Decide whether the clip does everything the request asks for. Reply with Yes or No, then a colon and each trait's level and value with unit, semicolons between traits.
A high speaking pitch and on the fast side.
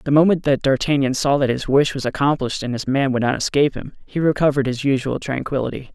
No: low, 135 Hz; fast, 220 wpm